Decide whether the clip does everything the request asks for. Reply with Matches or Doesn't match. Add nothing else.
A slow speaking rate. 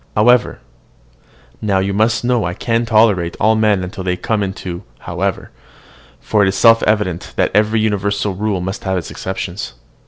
Doesn't match